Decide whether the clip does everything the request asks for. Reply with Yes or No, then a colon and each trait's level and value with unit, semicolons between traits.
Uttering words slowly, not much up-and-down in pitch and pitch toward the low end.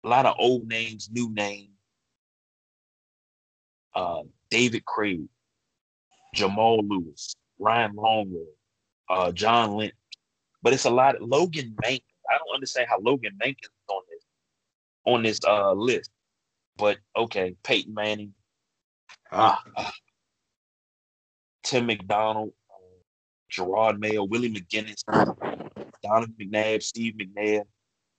Yes: slow, 110 wpm; narrow, 1.9 semitones; low, 110 Hz